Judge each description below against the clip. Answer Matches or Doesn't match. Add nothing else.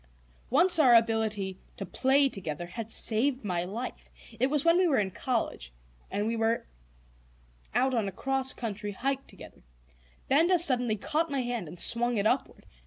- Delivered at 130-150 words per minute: Doesn't match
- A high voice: Matches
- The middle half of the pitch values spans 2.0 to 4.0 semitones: Doesn't match